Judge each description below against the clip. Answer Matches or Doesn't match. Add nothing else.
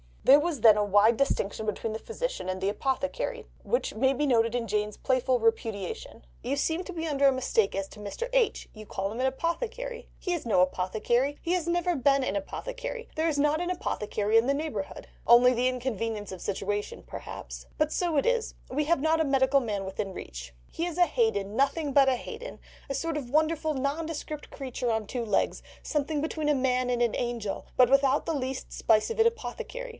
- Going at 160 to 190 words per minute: Doesn't match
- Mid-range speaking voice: Doesn't match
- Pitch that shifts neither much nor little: Doesn't match